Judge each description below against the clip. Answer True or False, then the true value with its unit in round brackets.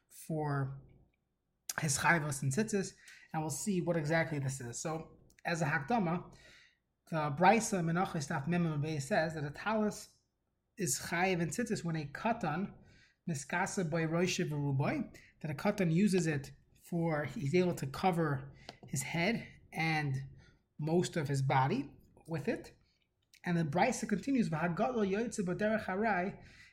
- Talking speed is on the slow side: True (130 wpm)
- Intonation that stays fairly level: False (4.1 semitones)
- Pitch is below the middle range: False (165 Hz)